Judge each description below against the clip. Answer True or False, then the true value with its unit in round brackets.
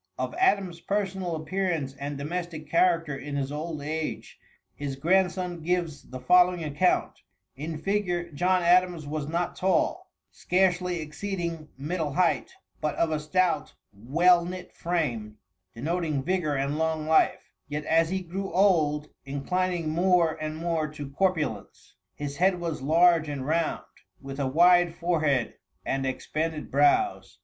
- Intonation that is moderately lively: True (3.5 semitones)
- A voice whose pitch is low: False (165 Hz)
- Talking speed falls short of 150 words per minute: True (140 wpm)